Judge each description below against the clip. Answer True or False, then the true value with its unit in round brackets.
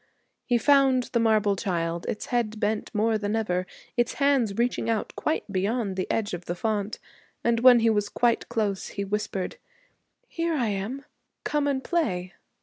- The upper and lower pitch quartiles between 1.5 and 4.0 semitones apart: True (3.5 semitones)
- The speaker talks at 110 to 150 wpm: False (170 wpm)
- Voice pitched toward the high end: True (220 Hz)